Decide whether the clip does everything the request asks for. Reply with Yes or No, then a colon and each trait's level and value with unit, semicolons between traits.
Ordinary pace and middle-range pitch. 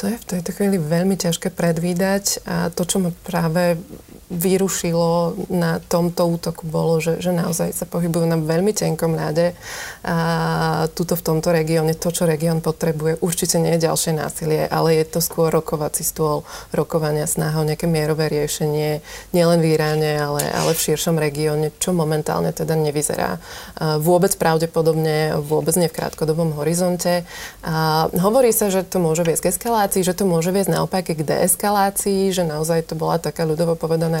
No: fast, 170 wpm; medium, 165 Hz